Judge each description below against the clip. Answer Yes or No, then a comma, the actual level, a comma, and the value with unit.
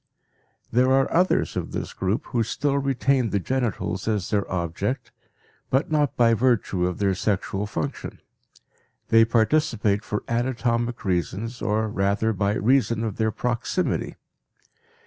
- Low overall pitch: Yes, low, 115 Hz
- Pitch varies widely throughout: No, average, 4.0 semitones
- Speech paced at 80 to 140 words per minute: Yes, slow, 135 wpm